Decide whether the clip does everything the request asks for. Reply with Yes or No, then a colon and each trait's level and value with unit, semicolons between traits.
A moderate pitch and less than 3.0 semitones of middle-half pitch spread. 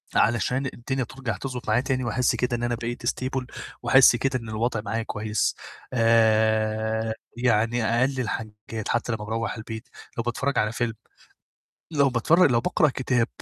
No: low, 120 Hz; narrow, 2.5 semitones